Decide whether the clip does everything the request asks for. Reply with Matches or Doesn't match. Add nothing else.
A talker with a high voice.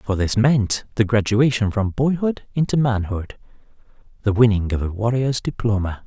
Doesn't match